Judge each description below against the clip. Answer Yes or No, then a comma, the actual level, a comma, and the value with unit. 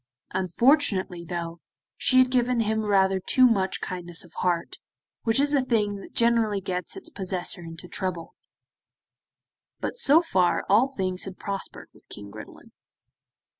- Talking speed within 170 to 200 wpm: No, average, 145 wpm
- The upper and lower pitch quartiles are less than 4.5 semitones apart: No, average, 5.1 semitones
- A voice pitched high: Yes, high, 195 Hz